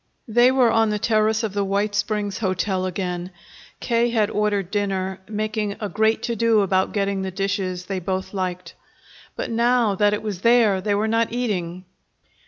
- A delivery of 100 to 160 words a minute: No, average, 180 wpm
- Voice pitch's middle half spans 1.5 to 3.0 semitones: Yes, narrow, 2.6 semitones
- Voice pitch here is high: Yes, high, 205 Hz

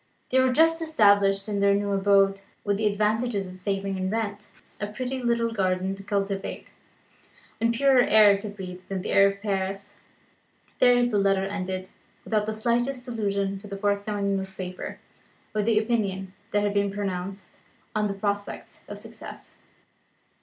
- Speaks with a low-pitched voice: No, high, 200 Hz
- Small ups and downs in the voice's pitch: Yes, narrow, 1.8 semitones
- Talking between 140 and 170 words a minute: Yes, average, 165 wpm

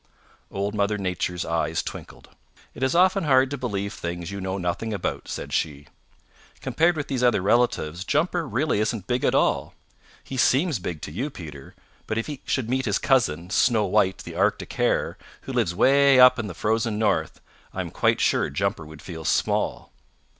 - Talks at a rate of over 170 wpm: Yes, average, 185 wpm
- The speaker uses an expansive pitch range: Yes, wide, 6.4 semitones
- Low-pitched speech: Yes, low, 110 Hz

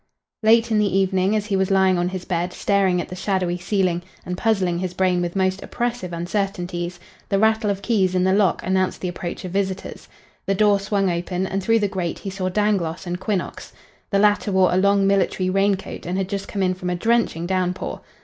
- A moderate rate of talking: No, fast, 215 wpm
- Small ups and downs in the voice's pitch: Yes, narrow, 1.7 semitones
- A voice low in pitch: No, high, 190 Hz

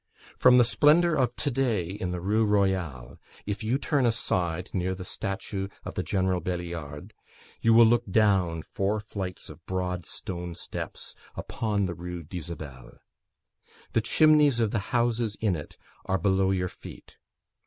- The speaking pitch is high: No, very low, 95 Hz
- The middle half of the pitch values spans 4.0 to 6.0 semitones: Yes, average, 4.4 semitones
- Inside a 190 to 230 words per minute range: No, average, 155 wpm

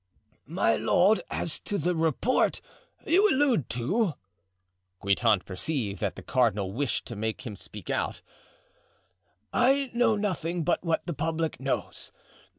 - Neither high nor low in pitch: Yes, medium, 145 Hz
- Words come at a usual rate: No, slow, 125 wpm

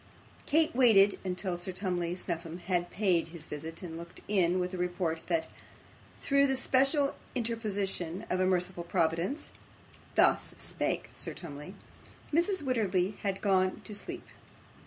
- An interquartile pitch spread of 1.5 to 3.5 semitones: No, average, 4.1 semitones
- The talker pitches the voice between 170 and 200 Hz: Yes, medium, 185 Hz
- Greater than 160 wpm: No, average, 140 wpm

